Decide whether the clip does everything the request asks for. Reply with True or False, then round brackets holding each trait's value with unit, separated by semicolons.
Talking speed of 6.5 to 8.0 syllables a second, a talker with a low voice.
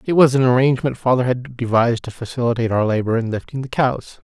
True (6.6 syllables/s; 125 Hz)